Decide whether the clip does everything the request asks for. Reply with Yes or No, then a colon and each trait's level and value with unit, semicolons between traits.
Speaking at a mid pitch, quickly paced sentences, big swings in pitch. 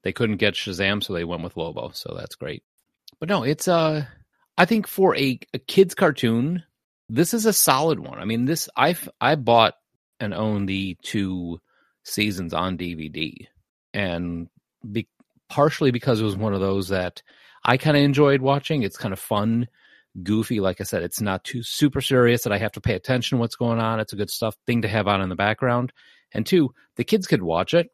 No: low, 115 Hz; fast, 210 wpm; wide, 6.3 semitones